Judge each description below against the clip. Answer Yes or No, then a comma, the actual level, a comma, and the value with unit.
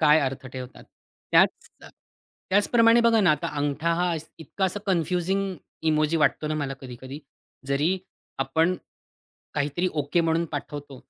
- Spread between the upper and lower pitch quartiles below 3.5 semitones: No, average, 4.3 semitones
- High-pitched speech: No, medium, 155 Hz